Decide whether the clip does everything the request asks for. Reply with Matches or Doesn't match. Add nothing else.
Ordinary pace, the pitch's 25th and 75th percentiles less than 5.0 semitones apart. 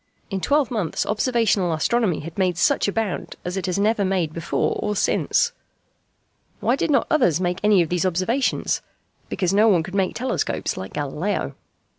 Matches